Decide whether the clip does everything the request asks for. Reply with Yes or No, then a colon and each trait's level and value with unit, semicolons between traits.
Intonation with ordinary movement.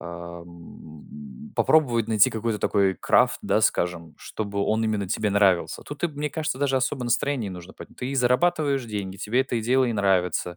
No: wide, 6.0 semitones